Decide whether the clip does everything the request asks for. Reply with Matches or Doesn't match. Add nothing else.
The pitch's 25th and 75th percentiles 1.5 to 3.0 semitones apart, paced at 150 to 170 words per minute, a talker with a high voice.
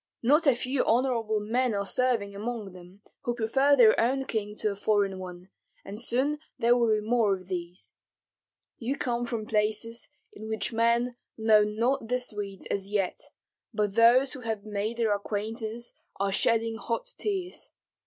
Matches